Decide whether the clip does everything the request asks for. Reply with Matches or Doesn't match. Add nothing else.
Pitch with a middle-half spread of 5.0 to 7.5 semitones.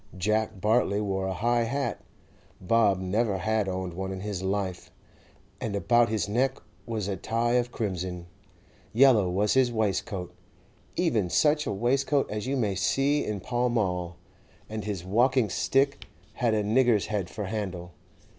Doesn't match